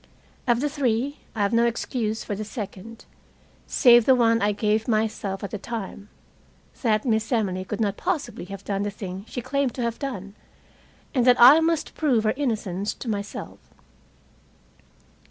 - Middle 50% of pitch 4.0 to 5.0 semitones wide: No, average, 3.3 semitones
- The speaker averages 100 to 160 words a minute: No, average, 170 wpm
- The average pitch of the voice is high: Yes, high, 225 Hz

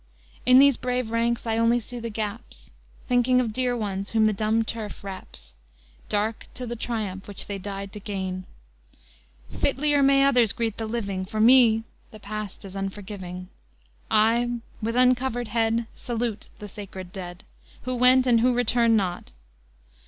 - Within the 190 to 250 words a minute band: No, average, 160 wpm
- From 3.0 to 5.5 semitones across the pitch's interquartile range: Yes, average, 3.3 semitones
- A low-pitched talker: No, high, 225 Hz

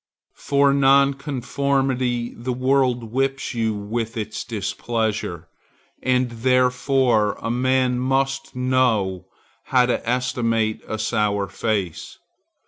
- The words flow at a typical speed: No, slow, 100 wpm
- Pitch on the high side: No, low, 125 Hz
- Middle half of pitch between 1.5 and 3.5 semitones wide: Yes, average, 2.9 semitones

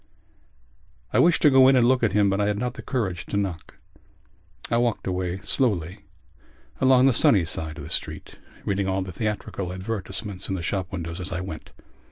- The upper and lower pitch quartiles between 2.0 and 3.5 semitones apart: No, average, 4.3 semitones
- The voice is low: Yes, low, 100 Hz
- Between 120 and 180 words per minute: No, average, 200 wpm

